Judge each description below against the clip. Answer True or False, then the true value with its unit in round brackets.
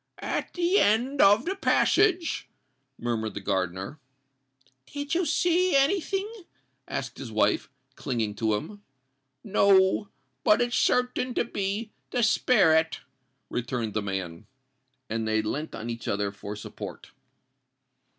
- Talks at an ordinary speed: False (125 wpm)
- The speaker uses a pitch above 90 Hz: True (190 Hz)